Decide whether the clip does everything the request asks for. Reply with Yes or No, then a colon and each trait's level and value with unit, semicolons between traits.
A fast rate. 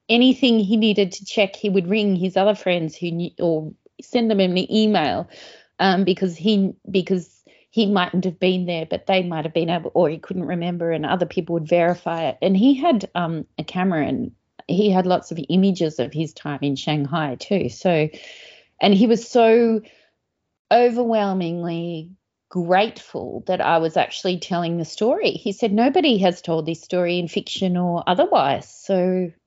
No: average, 175 wpm